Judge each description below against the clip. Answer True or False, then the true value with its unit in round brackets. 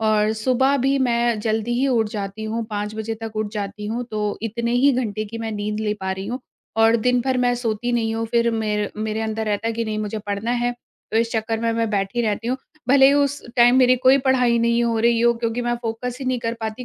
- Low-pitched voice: False (230 Hz)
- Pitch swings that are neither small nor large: False (2.1 semitones)